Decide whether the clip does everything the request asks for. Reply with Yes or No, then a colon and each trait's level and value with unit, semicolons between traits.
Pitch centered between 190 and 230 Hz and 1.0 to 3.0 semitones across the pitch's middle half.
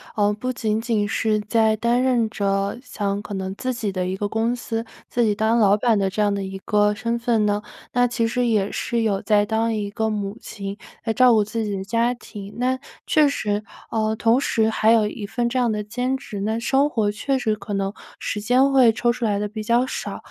Yes: high, 220 Hz; narrow, 2.5 semitones